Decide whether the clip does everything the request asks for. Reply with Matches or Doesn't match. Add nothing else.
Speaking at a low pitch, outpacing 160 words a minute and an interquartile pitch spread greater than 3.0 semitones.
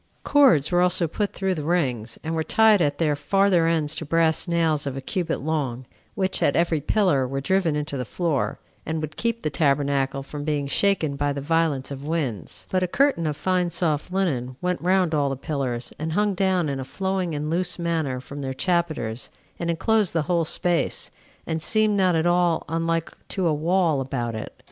Doesn't match